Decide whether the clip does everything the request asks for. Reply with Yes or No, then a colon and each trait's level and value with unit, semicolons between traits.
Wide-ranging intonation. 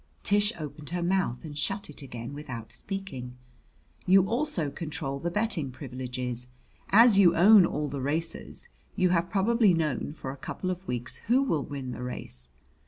Yes: wide, 6.7 semitones